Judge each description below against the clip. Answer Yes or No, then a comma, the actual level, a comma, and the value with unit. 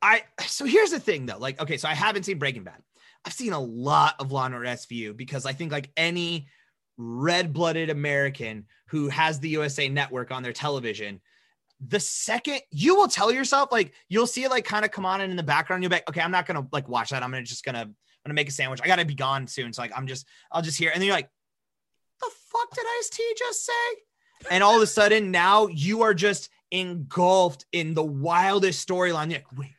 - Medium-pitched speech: Yes, medium, 160 Hz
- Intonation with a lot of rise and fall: Yes, wide, 7.2 semitones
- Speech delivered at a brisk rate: Yes, fast, 235 wpm